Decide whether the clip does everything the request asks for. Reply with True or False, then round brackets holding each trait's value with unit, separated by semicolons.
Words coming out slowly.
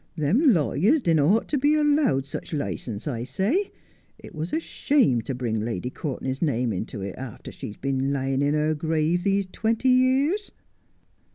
False (170 wpm)